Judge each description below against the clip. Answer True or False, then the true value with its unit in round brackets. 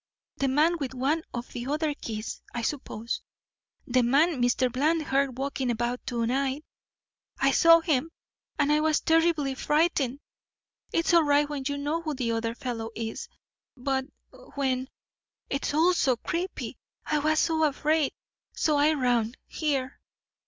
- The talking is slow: False (150 wpm)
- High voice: True (280 Hz)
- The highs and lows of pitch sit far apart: False (3.6 semitones)